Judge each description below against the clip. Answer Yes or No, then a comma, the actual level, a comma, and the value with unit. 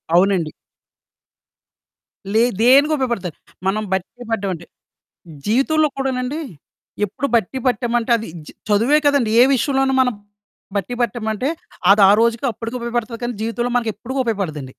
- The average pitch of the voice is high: Yes, high, 235 Hz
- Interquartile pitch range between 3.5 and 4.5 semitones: Yes, average, 3.8 semitones